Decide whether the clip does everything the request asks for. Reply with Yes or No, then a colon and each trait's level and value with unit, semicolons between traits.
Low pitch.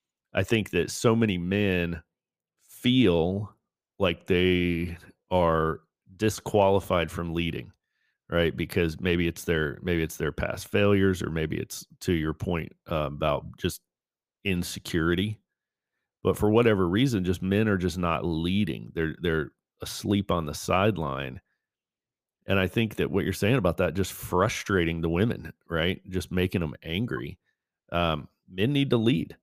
Yes: very low, 90 Hz